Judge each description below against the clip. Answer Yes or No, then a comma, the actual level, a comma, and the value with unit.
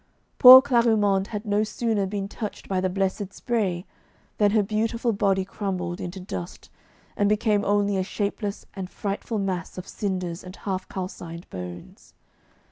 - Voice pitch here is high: Yes, high, 200 Hz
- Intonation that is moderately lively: No, narrow, 2.2 semitones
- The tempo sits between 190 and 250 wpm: No, average, 150 wpm